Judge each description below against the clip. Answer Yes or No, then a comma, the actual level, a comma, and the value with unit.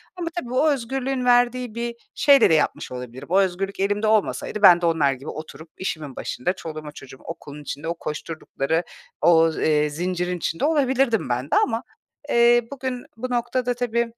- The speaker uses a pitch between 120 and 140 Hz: No, high, 195 Hz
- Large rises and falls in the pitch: Yes, wide, 7.6 semitones